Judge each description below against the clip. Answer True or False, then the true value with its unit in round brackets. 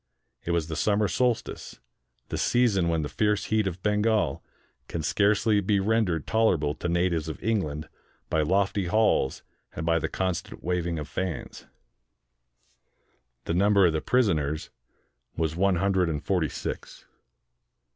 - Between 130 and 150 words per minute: True (145 wpm)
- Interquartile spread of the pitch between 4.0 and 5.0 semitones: True (4.3 semitones)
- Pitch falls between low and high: False (90 Hz)